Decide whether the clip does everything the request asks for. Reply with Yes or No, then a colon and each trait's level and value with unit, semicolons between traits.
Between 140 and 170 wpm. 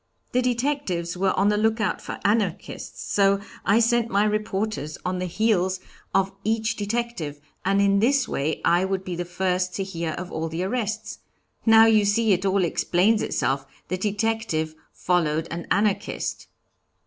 Yes: average, 160 wpm